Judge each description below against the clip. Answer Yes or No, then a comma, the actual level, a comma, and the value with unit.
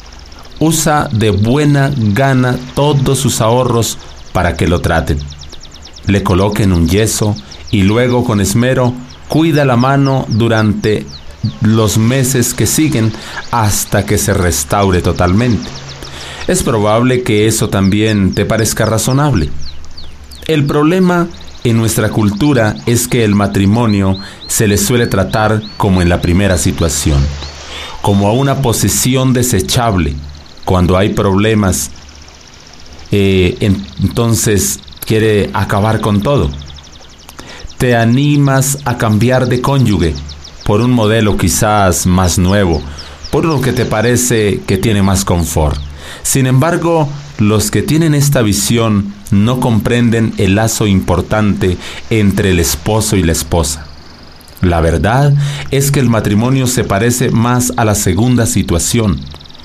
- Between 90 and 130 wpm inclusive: Yes, slow, 125 wpm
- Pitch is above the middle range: No, low, 105 Hz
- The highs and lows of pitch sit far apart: Yes, wide, 5.7 semitones